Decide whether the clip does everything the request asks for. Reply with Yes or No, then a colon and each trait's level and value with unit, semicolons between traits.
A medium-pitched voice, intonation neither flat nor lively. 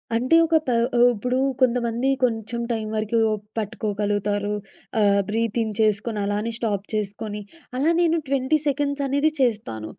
No: high, 225 Hz; average, 3.5 semitones